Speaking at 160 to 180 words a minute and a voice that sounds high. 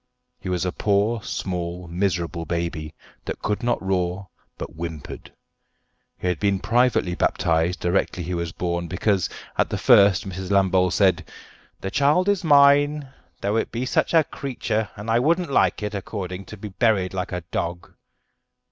No: average, 165 wpm; very low, 95 Hz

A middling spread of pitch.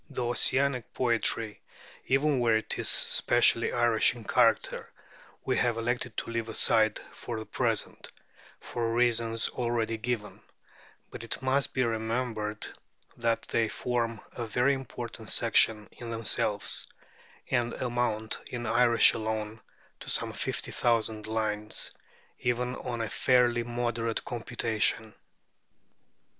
No: narrow, 1.6 semitones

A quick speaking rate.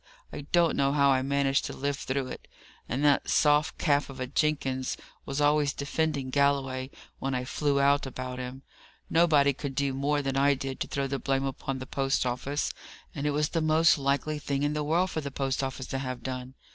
Yes: fast, 210 wpm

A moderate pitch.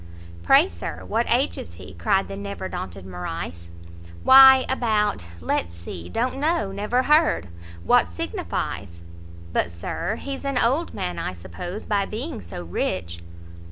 Yes: medium, 175 Hz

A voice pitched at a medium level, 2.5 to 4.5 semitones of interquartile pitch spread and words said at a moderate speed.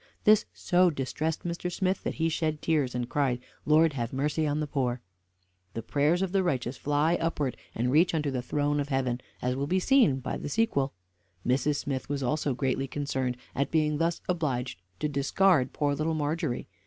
Yes: medium, 145 Hz; average, 3.6 semitones; average, 190 wpm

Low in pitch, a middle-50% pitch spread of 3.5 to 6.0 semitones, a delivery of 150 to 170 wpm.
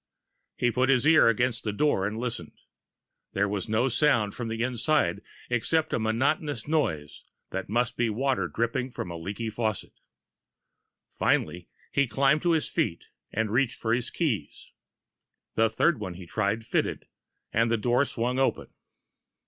Yes: low, 115 Hz; average, 3.9 semitones; average, 155 wpm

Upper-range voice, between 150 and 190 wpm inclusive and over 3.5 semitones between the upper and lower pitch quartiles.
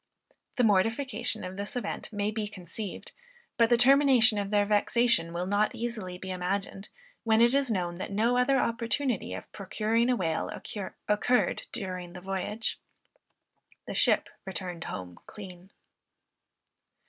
No: high, 210 Hz; average, 140 wpm; average, 4.1 semitones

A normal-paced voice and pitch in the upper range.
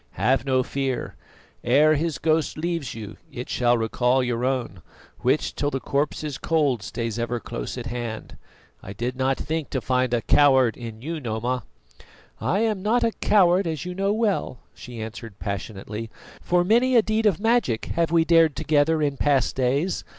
No: average, 180 wpm; low, 135 Hz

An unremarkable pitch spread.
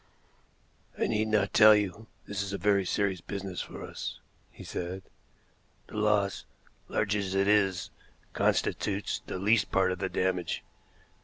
No: narrow, 1.8 semitones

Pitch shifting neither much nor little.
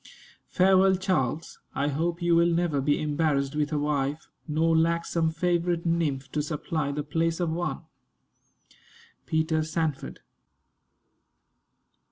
No: narrow, 2.3 semitones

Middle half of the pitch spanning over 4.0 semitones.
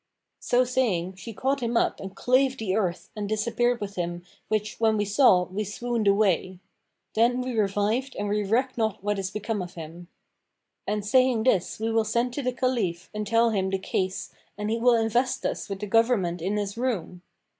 No: average, 3.6 semitones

